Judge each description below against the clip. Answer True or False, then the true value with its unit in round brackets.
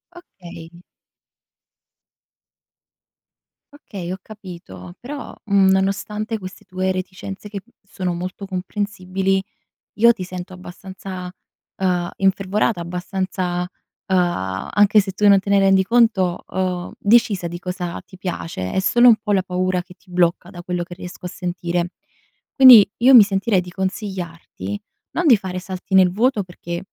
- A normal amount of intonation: False (2.1 semitones)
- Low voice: False (185 Hz)